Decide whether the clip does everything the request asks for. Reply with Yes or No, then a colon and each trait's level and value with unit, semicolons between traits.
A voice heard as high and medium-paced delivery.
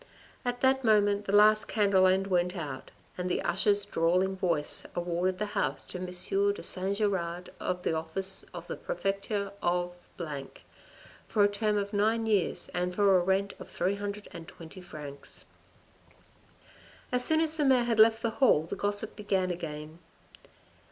Yes: high, 195 Hz; average, 160 wpm